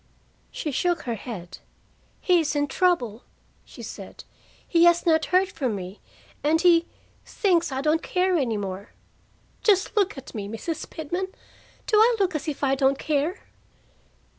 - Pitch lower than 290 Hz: No, very high, 315 Hz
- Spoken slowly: No, average, 160 wpm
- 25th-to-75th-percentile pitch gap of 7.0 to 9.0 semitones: No, wide, 5.4 semitones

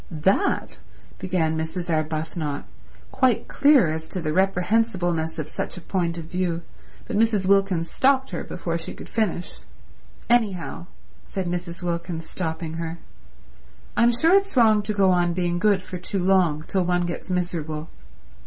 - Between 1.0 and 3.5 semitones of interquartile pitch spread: Yes, average, 3.2 semitones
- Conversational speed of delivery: Yes, average, 155 wpm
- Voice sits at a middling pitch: Yes, medium, 180 Hz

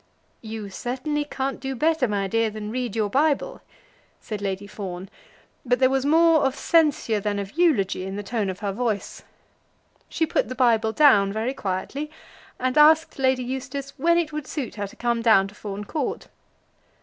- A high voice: Yes, high, 245 Hz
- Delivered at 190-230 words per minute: No, average, 180 wpm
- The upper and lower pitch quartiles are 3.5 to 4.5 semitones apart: No, wide, 5.4 semitones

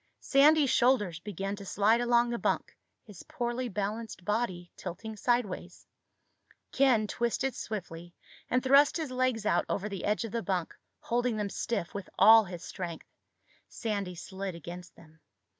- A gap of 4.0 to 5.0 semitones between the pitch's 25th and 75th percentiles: Yes, average, 4.4 semitones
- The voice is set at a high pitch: Yes, high, 210 Hz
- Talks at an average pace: Yes, average, 150 wpm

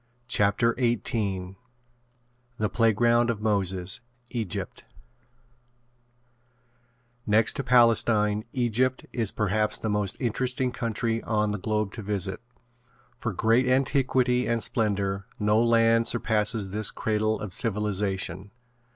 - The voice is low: Yes, low, 110 Hz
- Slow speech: Yes, slow, 110 wpm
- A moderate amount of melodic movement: No, narrow, 2.3 semitones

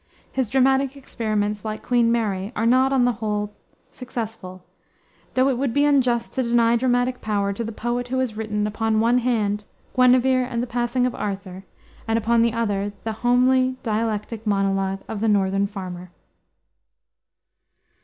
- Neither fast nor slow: Yes, average, 160 wpm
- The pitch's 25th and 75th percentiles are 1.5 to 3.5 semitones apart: Yes, average, 3.1 semitones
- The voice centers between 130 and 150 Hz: No, high, 230 Hz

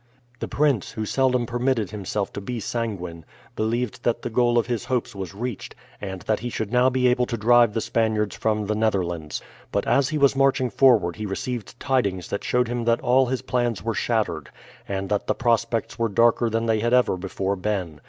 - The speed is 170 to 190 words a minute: No, fast, 205 wpm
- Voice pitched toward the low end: Yes, low, 115 Hz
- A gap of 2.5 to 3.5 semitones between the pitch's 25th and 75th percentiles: Yes, average, 3.2 semitones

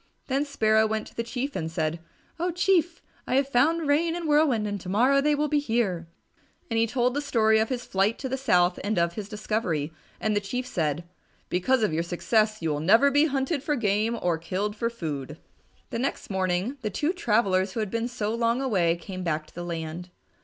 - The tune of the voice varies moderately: No, wide, 6.5 semitones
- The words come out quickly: Yes, fast, 215 wpm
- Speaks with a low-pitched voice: No, high, 220 Hz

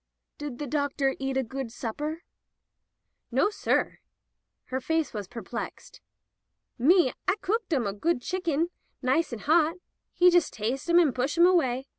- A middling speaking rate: Yes, average, 150 wpm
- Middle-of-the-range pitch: No, very high, 290 Hz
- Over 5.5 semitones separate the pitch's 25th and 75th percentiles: No, average, 5.2 semitones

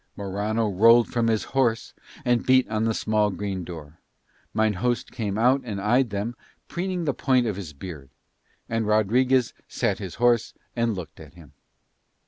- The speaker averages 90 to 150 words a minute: No, average, 165 wpm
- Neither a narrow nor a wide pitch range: Yes, average, 3.6 semitones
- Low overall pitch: Yes, low, 110 Hz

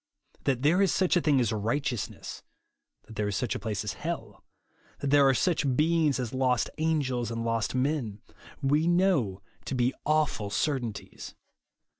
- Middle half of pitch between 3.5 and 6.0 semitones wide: Yes, average, 5.0 semitones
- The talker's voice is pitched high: No, low, 130 Hz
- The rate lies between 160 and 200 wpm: Yes, average, 165 wpm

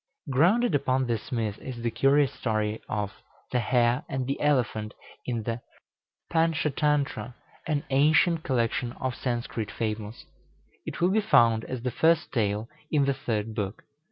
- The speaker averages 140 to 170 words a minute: Yes, average, 150 wpm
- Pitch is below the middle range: Yes, low, 125 Hz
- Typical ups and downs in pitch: Yes, average, 4.3 semitones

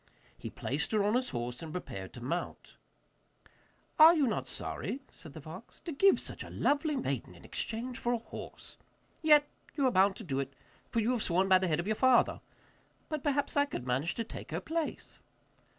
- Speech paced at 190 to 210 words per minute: Yes, fast, 205 wpm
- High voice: Yes, high, 225 Hz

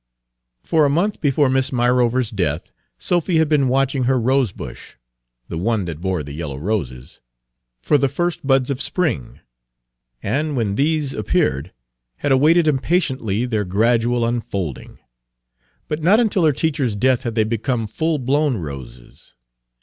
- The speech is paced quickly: No, average, 145 wpm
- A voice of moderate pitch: No, low, 125 Hz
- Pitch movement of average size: No, wide, 6.2 semitones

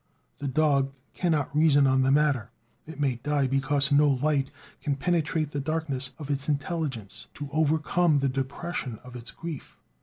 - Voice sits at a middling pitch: Yes, medium, 145 Hz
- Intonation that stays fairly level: Yes, narrow, 2.3 semitones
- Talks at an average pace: Yes, average, 160 wpm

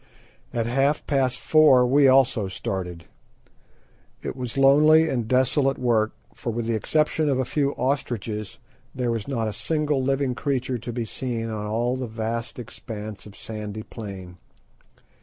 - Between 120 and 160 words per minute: Yes, average, 155 wpm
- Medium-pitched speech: No, low, 125 Hz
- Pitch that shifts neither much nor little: Yes, average, 3.7 semitones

